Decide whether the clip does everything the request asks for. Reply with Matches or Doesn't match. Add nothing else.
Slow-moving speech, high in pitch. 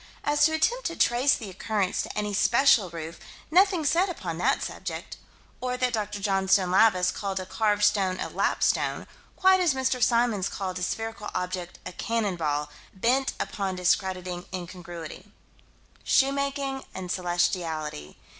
Doesn't match